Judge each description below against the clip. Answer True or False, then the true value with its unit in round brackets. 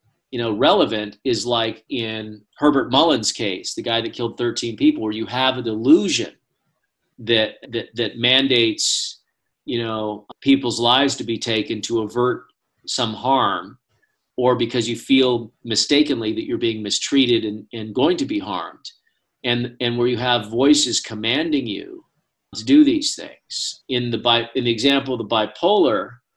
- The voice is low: True (120 Hz)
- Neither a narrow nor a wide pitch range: True (3.1 semitones)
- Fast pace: False (160 wpm)